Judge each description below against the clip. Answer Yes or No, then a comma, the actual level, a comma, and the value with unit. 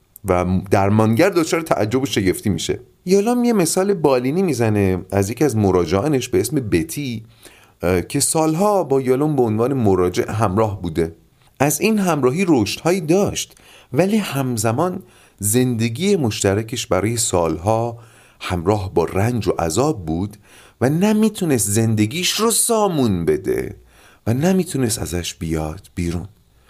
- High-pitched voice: No, low, 115 Hz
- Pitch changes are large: Yes, wide, 8.1 semitones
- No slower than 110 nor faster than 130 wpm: Yes, average, 125 wpm